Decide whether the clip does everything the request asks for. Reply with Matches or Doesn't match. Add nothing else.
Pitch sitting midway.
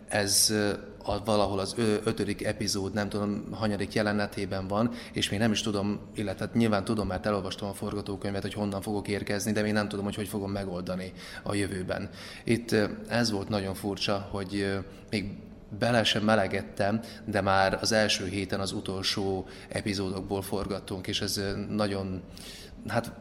Doesn't match